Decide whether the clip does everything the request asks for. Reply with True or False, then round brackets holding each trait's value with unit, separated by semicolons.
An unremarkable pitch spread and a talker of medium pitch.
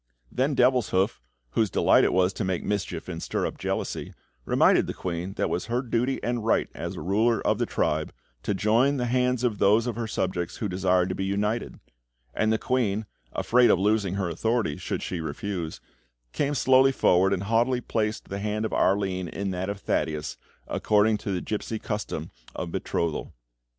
False (4.0 semitones; 105 Hz)